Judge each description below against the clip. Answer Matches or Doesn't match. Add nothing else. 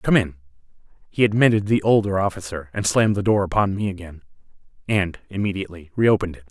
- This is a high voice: Doesn't match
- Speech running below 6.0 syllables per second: Doesn't match